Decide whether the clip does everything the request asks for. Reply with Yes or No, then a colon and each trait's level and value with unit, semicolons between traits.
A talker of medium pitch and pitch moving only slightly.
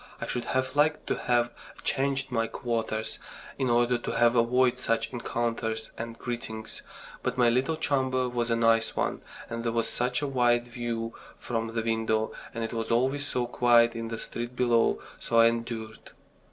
No: low, 120 Hz; narrow, 1.5 semitones